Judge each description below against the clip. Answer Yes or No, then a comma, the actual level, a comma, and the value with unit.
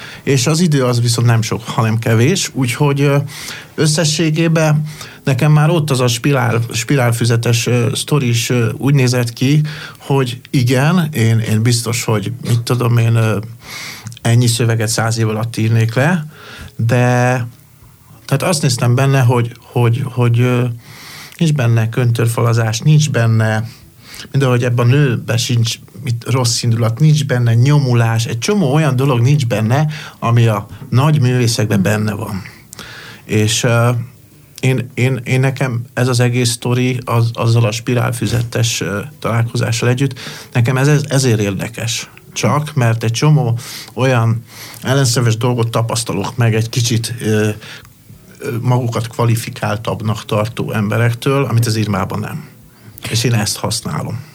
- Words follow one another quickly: No, average, 135 wpm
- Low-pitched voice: Yes, low, 120 Hz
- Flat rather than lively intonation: No, average, 3.1 semitones